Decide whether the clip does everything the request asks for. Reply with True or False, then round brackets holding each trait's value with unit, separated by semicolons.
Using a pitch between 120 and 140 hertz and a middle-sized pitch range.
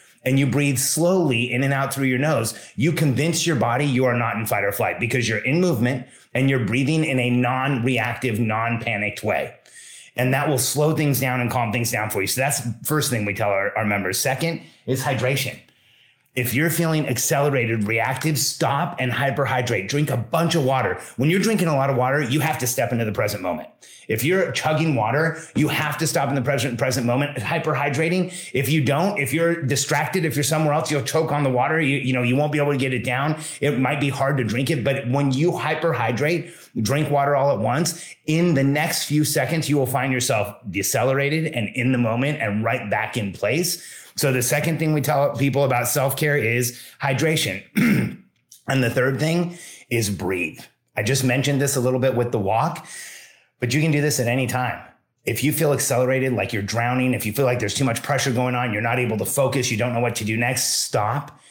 True (135 Hz; 3.5 semitones)